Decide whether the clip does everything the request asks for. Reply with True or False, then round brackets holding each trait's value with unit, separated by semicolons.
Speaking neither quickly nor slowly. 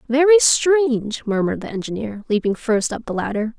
True (165 wpm)